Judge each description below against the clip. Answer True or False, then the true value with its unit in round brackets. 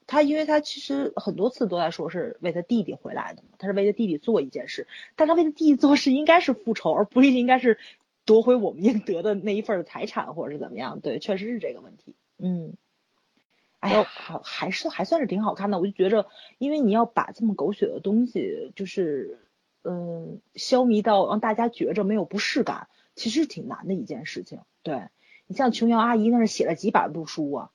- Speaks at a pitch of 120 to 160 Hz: False (225 Hz)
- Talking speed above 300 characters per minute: True (315 characters per minute)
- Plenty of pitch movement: False (4.8 semitones)